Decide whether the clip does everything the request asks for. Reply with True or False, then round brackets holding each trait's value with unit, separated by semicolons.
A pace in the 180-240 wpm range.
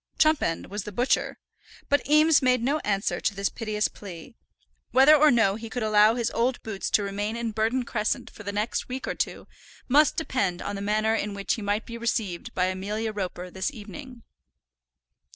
True (190 wpm)